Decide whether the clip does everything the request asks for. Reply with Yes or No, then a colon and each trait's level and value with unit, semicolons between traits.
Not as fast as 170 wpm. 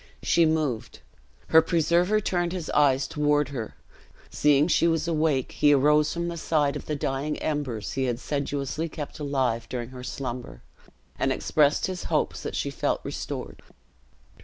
Yes: average, 160 wpm